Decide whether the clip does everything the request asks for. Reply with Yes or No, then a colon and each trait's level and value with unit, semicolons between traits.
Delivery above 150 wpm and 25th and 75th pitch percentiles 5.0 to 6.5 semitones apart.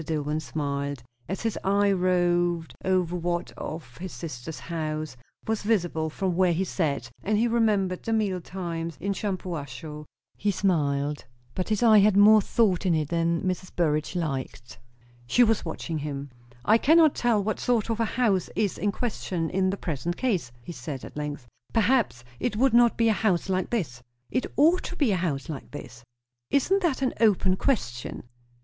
Yes: average, 180 wpm; wide, 5.5 semitones